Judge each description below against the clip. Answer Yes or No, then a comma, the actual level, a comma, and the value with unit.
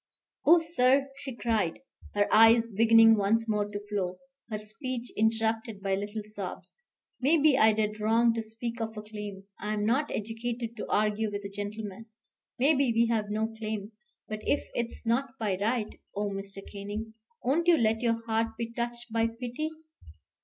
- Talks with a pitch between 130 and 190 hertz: No, high, 225 Hz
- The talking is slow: No, average, 165 wpm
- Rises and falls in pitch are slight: Yes, narrow, 2.1 semitones